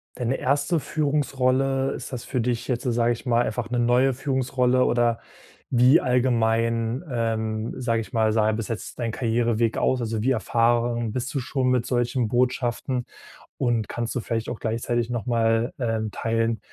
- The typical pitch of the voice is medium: No, low, 120 Hz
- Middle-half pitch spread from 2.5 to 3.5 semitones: No, narrow, 2.0 semitones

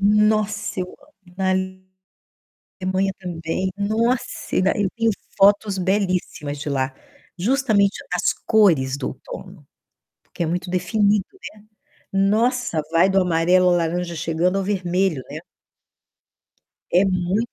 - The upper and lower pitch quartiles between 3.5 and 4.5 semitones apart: No, average, 2.8 semitones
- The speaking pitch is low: No, medium, 185 Hz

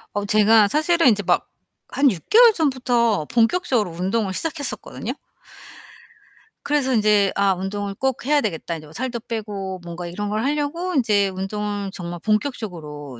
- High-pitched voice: Yes, high, 210 Hz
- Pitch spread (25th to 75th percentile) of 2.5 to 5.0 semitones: No, wide, 5.4 semitones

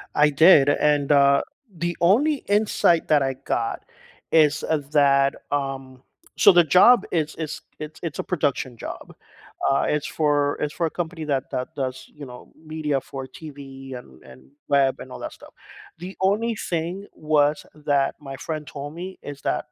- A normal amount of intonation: Yes, average, 3.0 semitones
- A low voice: No, medium, 150 Hz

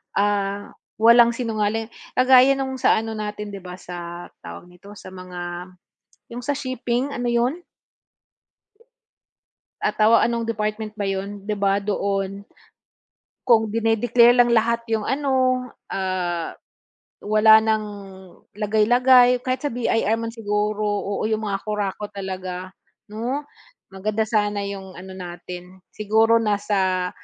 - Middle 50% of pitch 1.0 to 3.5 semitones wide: Yes, average, 3.0 semitones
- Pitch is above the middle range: Yes, high, 215 Hz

